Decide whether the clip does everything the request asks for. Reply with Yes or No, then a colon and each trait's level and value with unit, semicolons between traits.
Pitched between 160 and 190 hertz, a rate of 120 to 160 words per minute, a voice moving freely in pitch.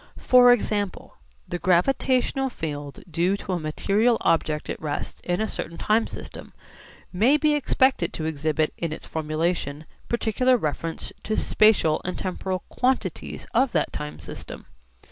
Yes: medium, 185 Hz; average, 145 wpm; wide, 7.0 semitones